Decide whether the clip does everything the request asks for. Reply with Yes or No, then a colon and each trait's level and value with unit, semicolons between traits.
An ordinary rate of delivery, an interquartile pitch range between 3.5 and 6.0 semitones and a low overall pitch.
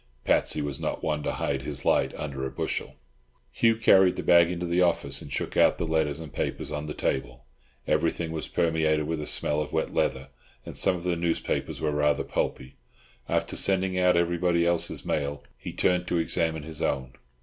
No: average, 195 wpm; average, 2.9 semitones; very low, 80 Hz